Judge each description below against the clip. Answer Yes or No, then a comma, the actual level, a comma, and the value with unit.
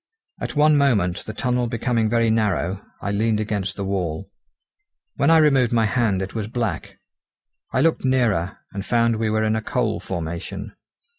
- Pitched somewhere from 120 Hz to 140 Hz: No, low, 110 Hz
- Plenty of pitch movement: No, average, 3.5 semitones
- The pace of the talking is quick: No, average, 170 wpm